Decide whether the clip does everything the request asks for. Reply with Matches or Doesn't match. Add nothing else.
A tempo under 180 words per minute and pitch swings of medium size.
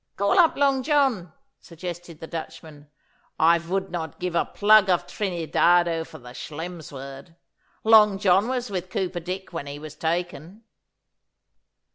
Matches